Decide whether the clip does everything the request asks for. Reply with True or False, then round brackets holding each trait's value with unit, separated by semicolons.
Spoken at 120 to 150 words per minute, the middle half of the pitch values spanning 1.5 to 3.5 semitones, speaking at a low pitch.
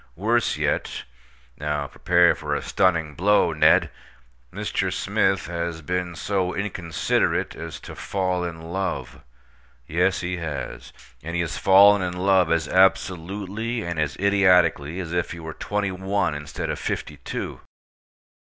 True (140 wpm; 2.9 semitones; 90 Hz)